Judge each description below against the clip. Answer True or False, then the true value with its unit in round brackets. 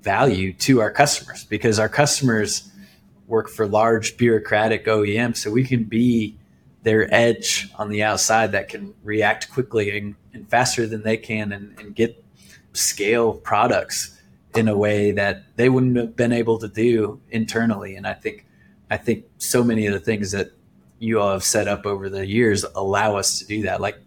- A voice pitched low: True (110 Hz)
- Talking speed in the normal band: True (180 wpm)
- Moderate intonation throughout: False (1.9 semitones)